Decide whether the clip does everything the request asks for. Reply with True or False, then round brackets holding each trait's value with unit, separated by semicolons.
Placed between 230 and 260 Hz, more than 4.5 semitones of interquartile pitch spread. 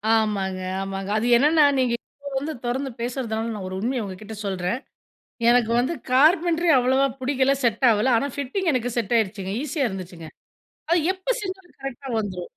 True (245 Hz; 5.3 semitones)